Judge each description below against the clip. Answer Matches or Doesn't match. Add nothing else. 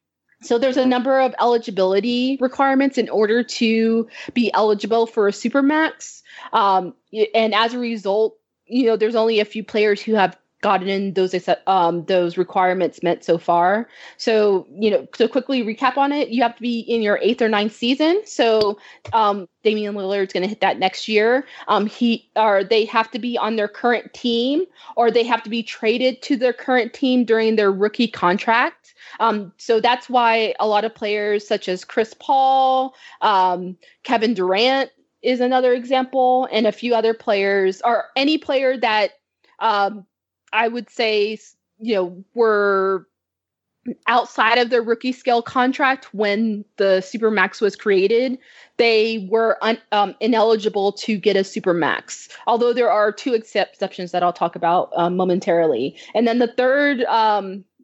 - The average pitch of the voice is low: Doesn't match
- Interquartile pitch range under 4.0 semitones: Matches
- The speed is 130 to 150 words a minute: Doesn't match